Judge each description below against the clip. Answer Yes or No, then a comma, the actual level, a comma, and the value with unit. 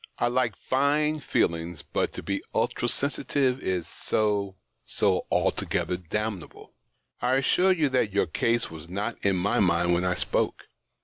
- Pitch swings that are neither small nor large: No, wide, 6.5 semitones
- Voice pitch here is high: No, low, 105 Hz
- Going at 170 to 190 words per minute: No, average, 150 wpm